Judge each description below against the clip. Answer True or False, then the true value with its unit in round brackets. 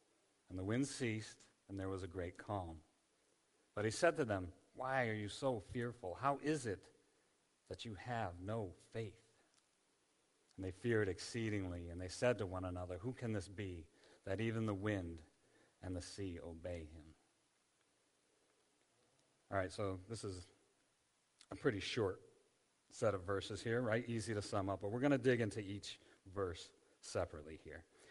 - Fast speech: False (165 wpm)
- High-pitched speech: False (105 Hz)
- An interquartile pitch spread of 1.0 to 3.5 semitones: False (4.0 semitones)